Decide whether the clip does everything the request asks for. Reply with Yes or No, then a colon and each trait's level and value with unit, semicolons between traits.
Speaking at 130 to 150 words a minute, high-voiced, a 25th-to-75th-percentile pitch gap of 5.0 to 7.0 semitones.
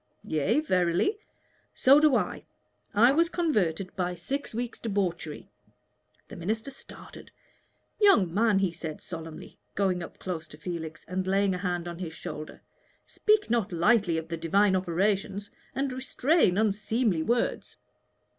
Yes: average, 140 wpm; high, 195 Hz; wide, 5.6 semitones